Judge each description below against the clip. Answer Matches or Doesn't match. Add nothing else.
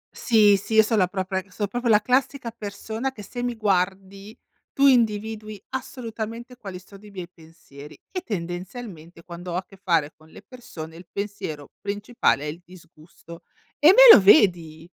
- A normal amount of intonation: Matches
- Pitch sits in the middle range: Doesn't match